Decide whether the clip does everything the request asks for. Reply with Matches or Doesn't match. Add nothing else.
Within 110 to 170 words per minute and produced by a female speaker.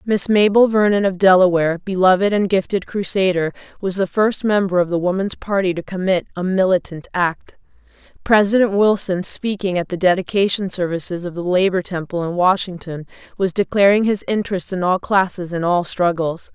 Matches